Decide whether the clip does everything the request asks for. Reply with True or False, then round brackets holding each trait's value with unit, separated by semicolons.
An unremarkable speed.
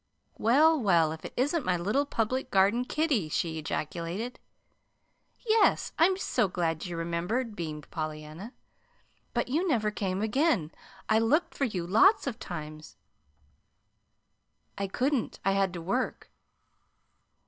False (130 wpm)